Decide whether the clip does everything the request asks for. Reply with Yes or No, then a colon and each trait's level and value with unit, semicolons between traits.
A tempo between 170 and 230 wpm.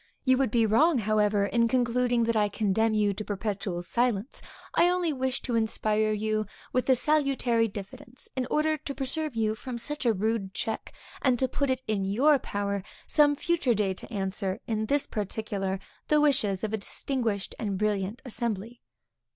Yes: average, 175 wpm